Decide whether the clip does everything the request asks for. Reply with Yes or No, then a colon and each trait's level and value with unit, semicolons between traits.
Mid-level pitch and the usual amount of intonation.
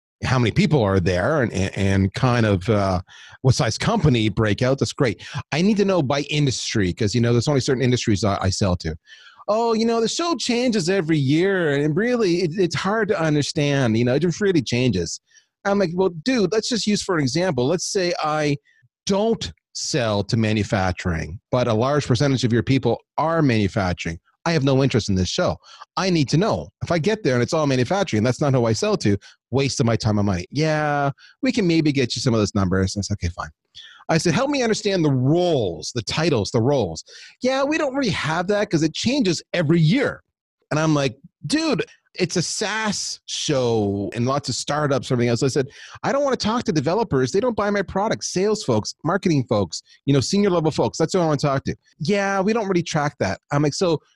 No: medium, 145 Hz; wide, 8.1 semitones